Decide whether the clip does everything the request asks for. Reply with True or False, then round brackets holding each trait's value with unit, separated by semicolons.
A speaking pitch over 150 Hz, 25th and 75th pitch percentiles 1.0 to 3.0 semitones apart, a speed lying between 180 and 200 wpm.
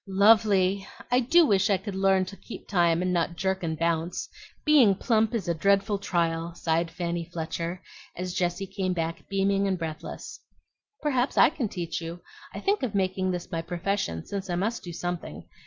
True (185 Hz; 2.7 semitones; 190 wpm)